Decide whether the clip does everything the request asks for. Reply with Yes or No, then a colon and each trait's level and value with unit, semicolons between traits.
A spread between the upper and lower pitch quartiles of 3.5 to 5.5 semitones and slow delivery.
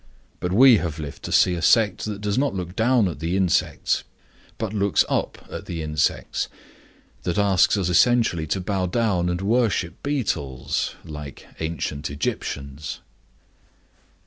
No: average, 4.8 semitones; average, 145 wpm